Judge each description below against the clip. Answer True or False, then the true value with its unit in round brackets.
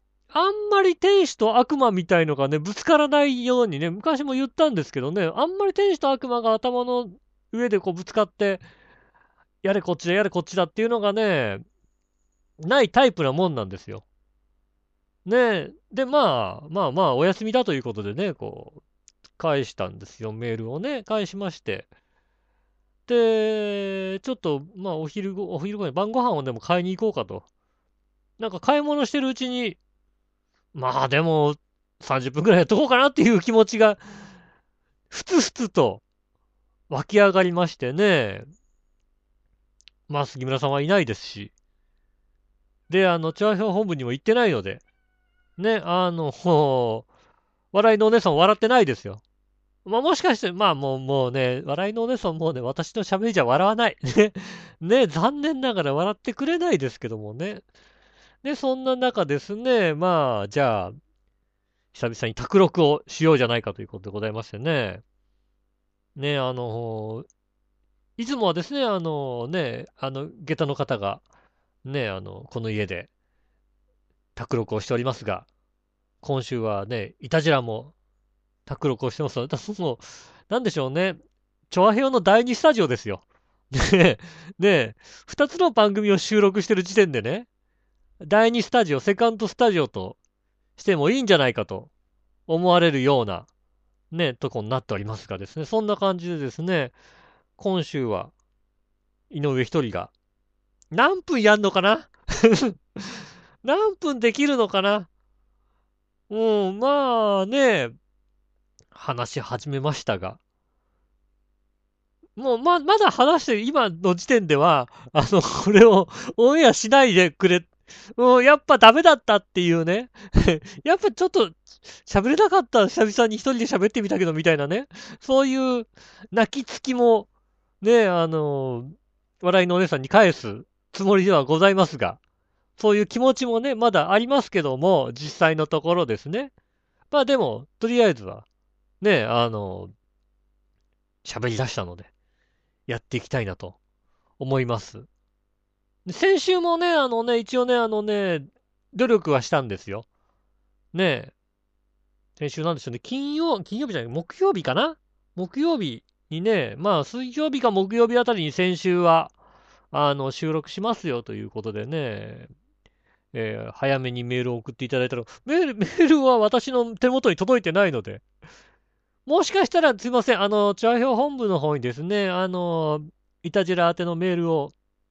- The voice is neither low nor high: True (180 Hz)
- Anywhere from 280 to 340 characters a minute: True (295 characters per minute)